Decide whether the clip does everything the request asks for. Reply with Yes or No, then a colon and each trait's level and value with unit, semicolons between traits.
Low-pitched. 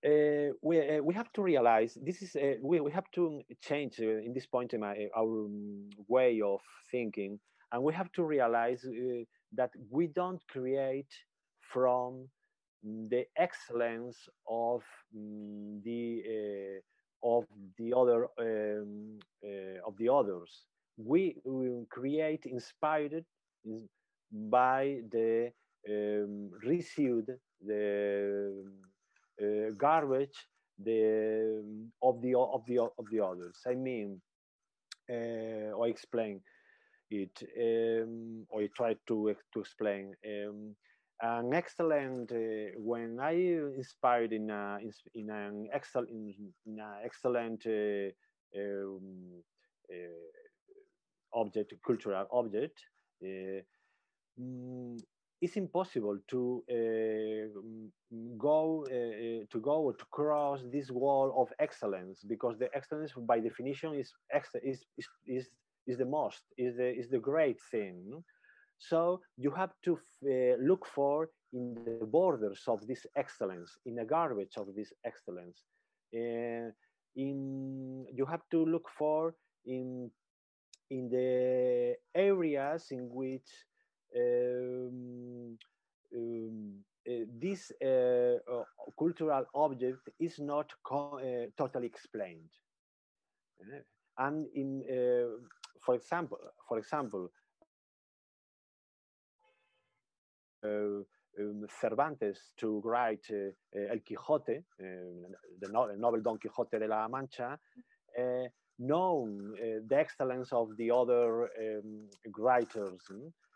Yes: low, 120 Hz